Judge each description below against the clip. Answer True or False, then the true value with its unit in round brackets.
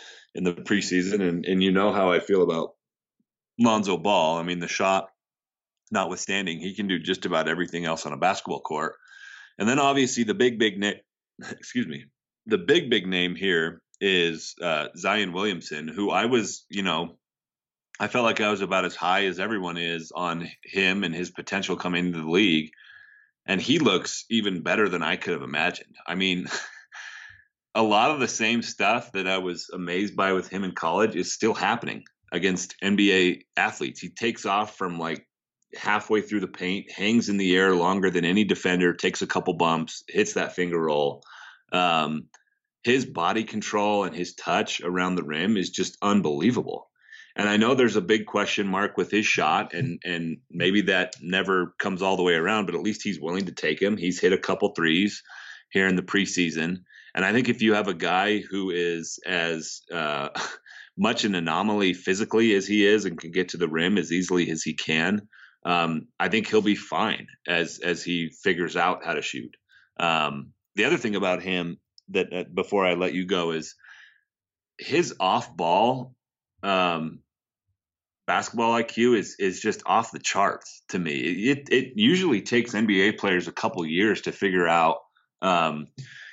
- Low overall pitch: True (95 Hz)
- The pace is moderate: True (185 wpm)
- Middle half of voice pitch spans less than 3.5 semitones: True (3.0 semitones)